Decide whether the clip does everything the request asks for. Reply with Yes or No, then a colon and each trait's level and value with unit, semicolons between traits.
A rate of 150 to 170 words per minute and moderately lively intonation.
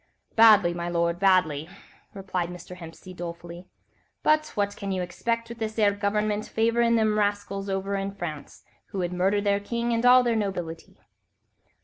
Yes: average, 160 wpm; average, 3.5 semitones